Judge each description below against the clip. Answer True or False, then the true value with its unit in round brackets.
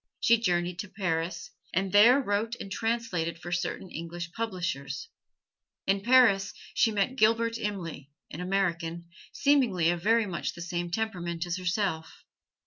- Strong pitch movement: False (4.4 semitones)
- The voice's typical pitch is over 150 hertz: True (190 Hz)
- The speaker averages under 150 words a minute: True (140 wpm)